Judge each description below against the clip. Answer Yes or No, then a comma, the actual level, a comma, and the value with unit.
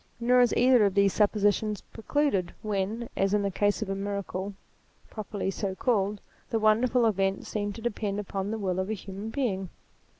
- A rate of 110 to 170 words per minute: No, average, 180 wpm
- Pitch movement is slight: Yes, narrow, 2.3 semitones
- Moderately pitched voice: No, high, 205 Hz